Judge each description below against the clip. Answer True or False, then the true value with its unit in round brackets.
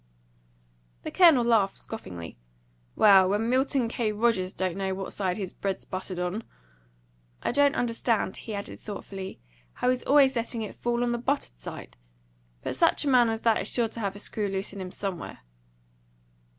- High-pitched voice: True (215 Hz)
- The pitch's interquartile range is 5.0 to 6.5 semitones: False (3.8 semitones)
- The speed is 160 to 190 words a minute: True (175 wpm)